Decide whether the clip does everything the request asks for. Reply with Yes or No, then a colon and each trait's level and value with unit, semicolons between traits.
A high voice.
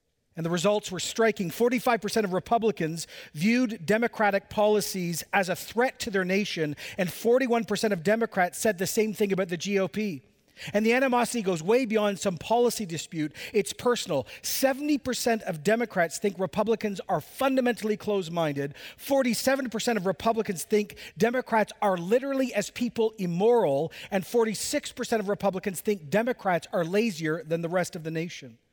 Yes: high, 210 Hz